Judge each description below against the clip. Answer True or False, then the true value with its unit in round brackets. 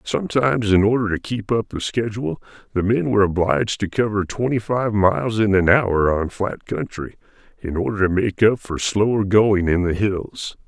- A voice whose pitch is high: False (105 Hz)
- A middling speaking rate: True (190 wpm)